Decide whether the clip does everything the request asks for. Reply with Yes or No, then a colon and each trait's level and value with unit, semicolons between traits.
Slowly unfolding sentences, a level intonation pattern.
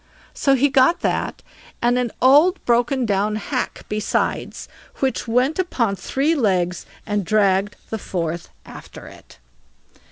No: slow, 130 wpm; average, 5.0 semitones